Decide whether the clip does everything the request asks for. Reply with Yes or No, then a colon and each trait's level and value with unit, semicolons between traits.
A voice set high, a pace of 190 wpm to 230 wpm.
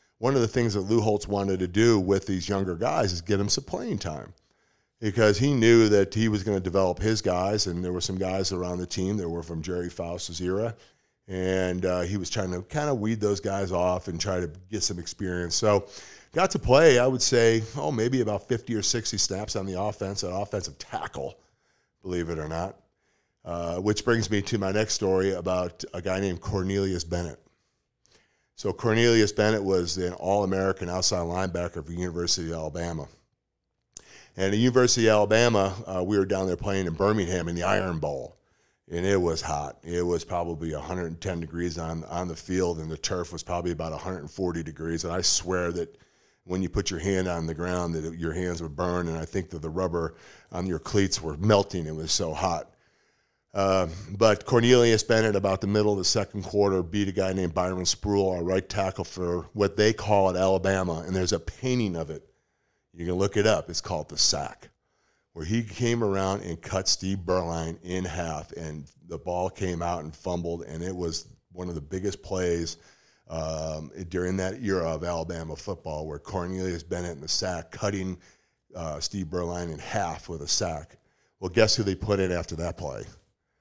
No: very low, 95 Hz; fast, 205 wpm